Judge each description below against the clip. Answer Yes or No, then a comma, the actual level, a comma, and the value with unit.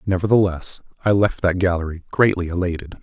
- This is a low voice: Yes, very low, 90 Hz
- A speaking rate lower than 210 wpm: Yes, average, 140 wpm